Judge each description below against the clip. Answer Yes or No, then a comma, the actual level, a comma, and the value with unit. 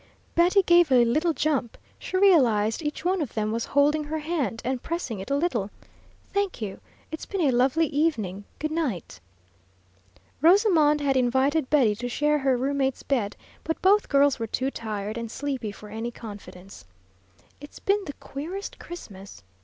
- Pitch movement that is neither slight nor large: No, wide, 5.9 semitones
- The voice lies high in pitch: Yes, very high, 275 Hz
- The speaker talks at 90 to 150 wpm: No, average, 160 wpm